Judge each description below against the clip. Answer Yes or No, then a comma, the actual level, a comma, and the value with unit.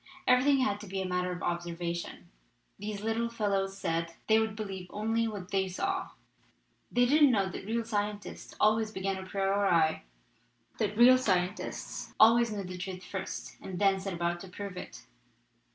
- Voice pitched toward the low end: No, high, 200 Hz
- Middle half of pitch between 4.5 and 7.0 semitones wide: No, average, 3.4 semitones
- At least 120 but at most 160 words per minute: No, average, 175 wpm